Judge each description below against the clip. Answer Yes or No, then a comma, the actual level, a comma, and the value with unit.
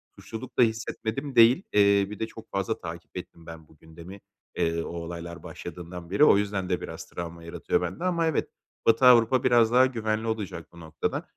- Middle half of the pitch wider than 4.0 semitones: Yes, wide, 5.4 semitones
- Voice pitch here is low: Yes, low, 100 Hz